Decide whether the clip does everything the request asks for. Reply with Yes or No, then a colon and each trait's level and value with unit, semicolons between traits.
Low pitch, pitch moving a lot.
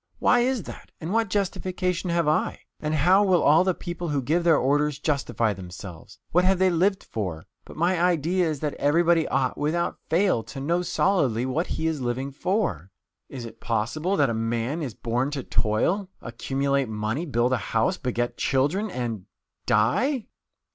No: medium, 150 Hz; wide, 6.7 semitones